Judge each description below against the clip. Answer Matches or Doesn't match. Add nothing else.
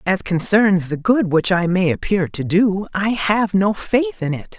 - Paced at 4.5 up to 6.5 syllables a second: Doesn't match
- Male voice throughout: Doesn't match